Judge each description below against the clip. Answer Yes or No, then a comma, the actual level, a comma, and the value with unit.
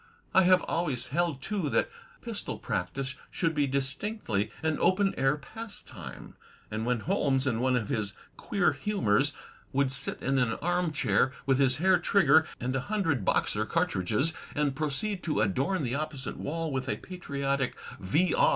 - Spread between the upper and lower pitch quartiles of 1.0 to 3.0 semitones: No, average, 4.9 semitones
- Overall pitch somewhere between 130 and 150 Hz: Yes, medium, 140 Hz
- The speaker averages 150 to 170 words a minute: Yes, average, 160 wpm